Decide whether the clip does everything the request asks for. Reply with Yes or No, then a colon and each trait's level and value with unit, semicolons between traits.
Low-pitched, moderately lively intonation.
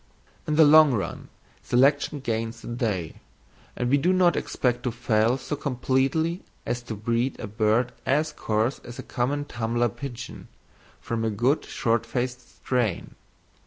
Yes: low, 125 Hz; average, 3.5 semitones